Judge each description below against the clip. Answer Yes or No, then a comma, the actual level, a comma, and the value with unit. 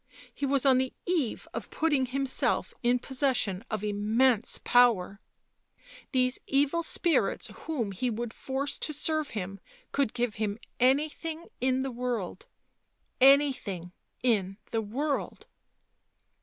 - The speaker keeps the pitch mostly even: No, average, 4.3 semitones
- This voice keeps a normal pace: No, slow, 130 wpm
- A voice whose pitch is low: No, very high, 255 Hz